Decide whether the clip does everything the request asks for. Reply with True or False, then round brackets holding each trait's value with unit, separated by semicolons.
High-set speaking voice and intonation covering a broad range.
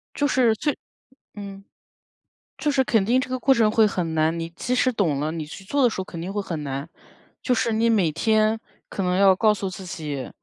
True (200 Hz; 5.7 semitones)